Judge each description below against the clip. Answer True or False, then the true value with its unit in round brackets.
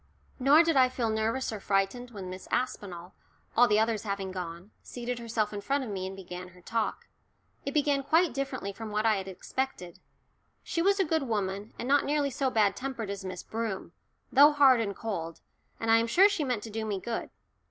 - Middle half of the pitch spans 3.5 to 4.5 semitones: False (5.1 semitones)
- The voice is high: True (225 Hz)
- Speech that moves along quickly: True (210 wpm)